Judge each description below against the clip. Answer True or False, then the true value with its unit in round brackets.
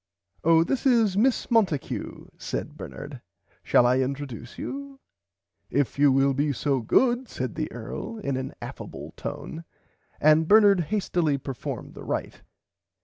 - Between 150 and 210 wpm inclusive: False (140 wpm)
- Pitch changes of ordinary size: False (7.9 semitones)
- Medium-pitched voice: True (155 Hz)